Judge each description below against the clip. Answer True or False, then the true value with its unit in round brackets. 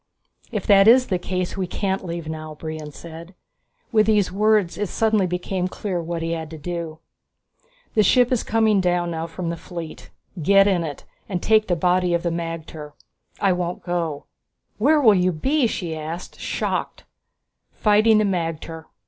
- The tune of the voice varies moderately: True (3.7 semitones)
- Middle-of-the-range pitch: True (180 Hz)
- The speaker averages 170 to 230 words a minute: True (175 wpm)